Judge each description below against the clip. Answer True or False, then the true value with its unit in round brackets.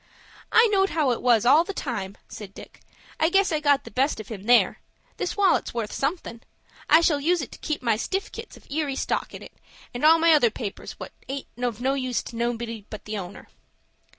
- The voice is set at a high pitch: True (265 Hz)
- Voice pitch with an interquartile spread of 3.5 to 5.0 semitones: False (5.6 semitones)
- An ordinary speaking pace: False (210 wpm)